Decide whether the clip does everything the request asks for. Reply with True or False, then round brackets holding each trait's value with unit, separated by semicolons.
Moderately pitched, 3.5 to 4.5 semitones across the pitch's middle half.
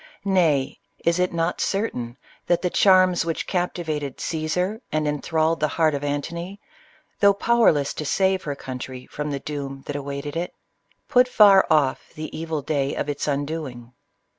True (155 Hz; 4.1 semitones)